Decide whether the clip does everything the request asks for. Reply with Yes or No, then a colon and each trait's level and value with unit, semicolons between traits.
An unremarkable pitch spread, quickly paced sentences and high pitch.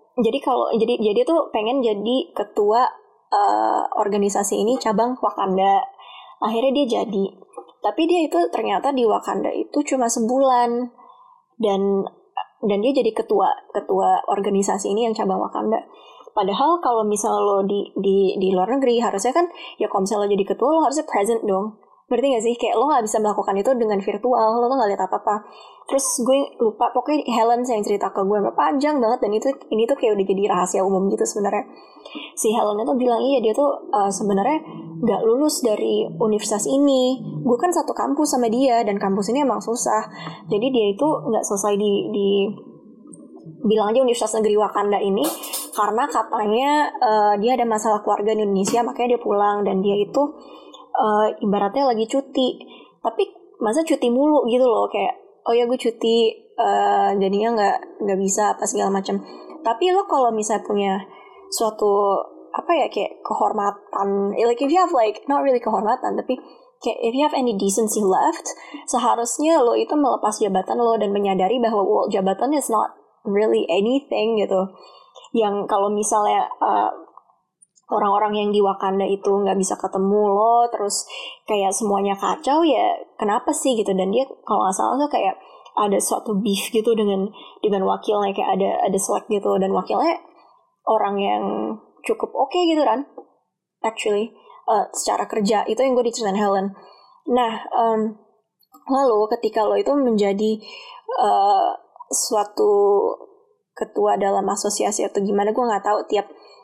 Yes: average, 4.8 semitones; fast, 165 wpm; high, 225 Hz